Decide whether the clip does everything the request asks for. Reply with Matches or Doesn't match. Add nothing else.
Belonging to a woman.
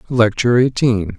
Doesn't match